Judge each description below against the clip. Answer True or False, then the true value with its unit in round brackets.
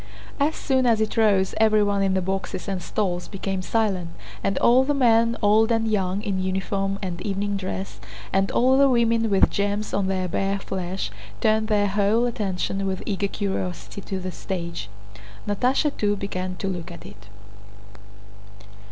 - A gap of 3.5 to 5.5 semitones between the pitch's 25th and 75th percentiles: False (2.6 semitones)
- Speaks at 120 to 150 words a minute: False (165 wpm)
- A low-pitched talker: False (200 Hz)